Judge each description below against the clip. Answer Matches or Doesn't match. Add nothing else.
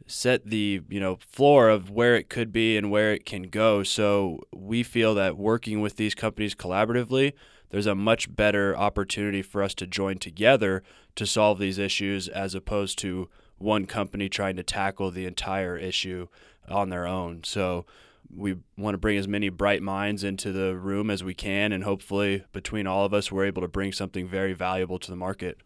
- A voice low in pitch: Matches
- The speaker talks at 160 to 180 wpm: Doesn't match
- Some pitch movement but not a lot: Doesn't match